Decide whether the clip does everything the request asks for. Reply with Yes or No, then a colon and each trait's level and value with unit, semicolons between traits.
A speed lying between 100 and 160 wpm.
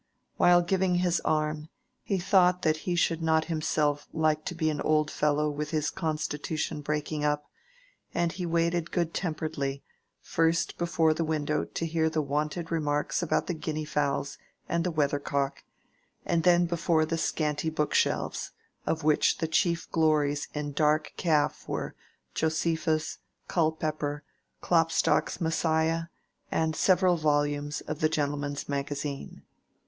Yes: average, 145 wpm